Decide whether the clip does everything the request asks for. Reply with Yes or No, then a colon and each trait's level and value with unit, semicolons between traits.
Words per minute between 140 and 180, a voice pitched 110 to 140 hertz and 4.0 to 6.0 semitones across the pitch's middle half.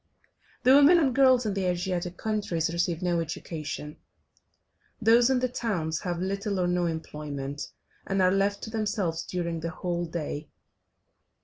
No: average, 150 wpm; medium, 180 Hz; average, 4.5 semitones